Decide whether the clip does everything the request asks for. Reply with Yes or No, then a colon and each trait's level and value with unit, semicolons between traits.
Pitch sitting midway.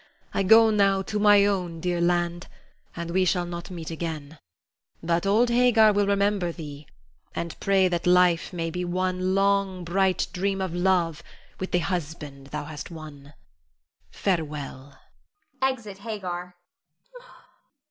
Yes: medium, 180 Hz